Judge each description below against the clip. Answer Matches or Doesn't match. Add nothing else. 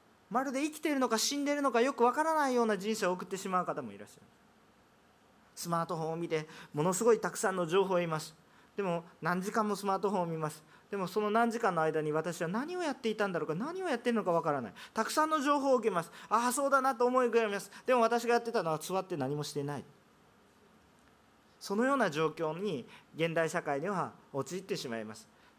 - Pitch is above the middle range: Matches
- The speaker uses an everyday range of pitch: Doesn't match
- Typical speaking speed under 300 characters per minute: Doesn't match